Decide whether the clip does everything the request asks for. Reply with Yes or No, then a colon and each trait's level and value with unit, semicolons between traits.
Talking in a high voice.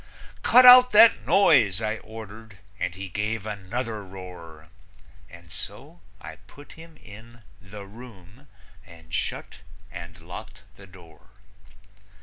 No: low, 100 Hz